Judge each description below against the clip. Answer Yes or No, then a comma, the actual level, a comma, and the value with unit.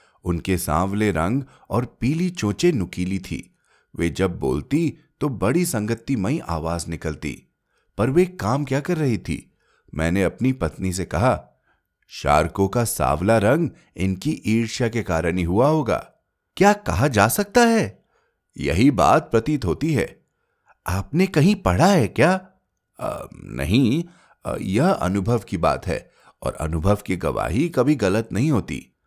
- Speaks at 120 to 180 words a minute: Yes, average, 140 wpm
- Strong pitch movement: Yes, wide, 8.7 semitones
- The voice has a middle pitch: No, low, 105 Hz